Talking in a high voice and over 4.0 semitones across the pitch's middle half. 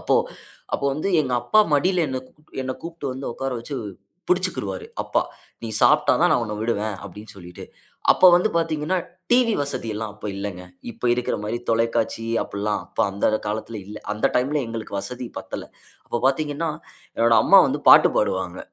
No: low, 120 Hz; wide, 5.6 semitones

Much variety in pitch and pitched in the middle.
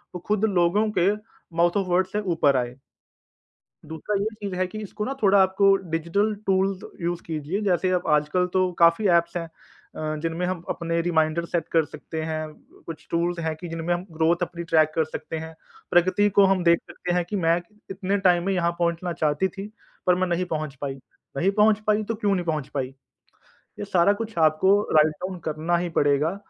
No: average, 3.0 semitones; medium, 175 Hz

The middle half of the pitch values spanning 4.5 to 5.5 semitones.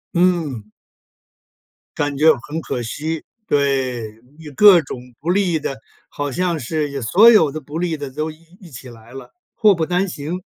No: average, 4.1 semitones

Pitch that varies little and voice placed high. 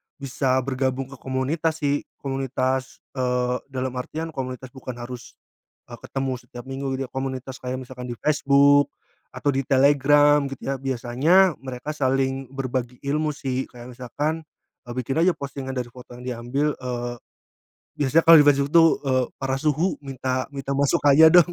No: narrow, 1.9 semitones; low, 135 Hz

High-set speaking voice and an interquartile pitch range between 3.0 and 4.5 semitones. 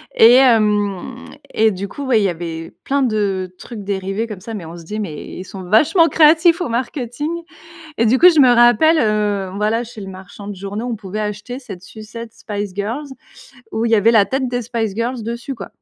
Yes: high, 220 Hz; average, 3.6 semitones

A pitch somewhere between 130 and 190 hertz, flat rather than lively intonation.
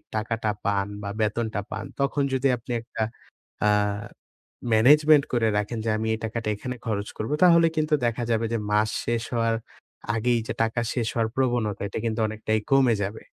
No: low, 115 Hz; narrow, 2.2 semitones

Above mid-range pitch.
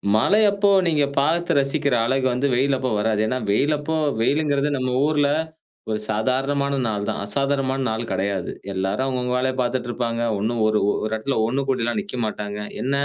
No: low, 130 Hz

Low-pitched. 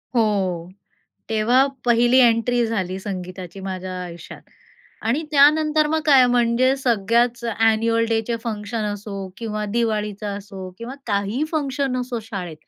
No: high, 225 Hz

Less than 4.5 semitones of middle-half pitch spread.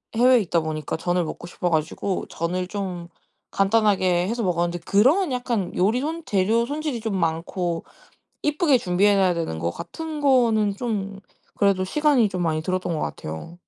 No: average, 5.2 semitones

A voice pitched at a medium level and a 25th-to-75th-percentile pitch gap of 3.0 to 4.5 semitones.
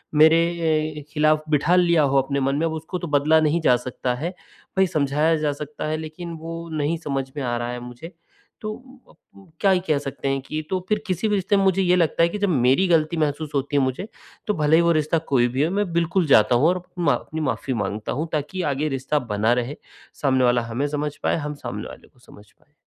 Yes: medium, 150 Hz; average, 3.6 semitones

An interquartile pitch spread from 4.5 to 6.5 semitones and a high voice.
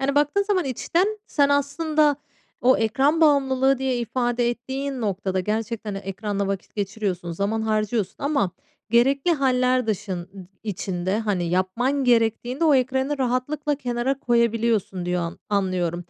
Yes: wide, 5.4 semitones; high, 240 Hz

